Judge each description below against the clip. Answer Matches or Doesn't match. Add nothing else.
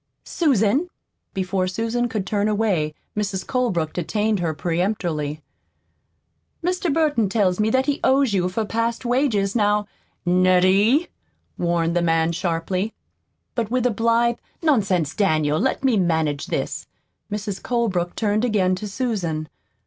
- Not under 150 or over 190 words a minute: Doesn't match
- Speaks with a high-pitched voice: Matches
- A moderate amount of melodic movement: Matches